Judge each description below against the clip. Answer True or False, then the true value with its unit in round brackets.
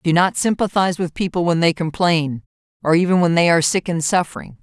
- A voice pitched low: False (170 Hz)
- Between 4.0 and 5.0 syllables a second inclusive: False (6.0 syllables/s)